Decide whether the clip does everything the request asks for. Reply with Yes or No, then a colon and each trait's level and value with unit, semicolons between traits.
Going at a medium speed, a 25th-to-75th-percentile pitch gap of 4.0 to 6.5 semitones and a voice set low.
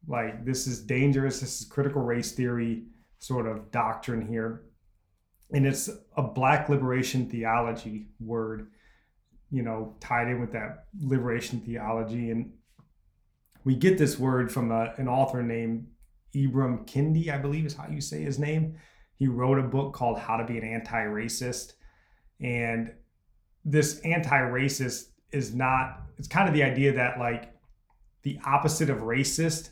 No: average, 155 wpm; average, 3.4 semitones; low, 125 Hz